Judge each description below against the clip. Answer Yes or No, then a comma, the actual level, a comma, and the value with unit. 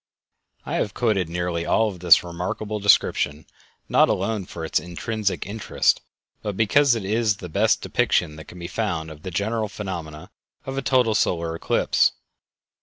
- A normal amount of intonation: Yes, average, 4.4 semitones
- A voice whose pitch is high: No, very low, 95 Hz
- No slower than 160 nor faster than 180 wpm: Yes, average, 165 wpm